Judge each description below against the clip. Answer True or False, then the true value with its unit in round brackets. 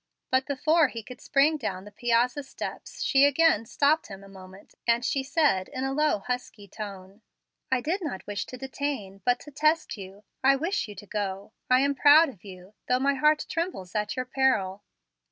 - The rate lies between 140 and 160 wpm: False (195 wpm)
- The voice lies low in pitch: False (250 Hz)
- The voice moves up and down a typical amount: False (5.9 semitones)